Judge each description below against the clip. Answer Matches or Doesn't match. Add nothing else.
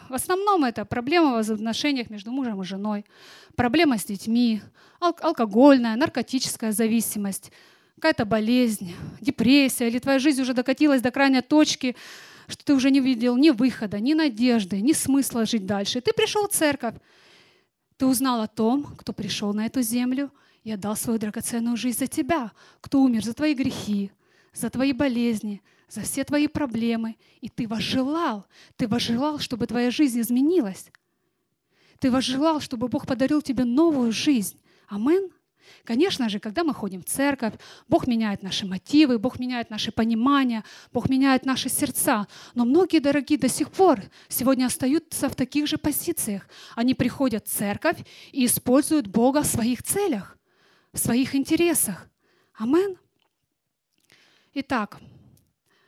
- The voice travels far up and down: Doesn't match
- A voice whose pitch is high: Matches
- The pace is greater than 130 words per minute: Matches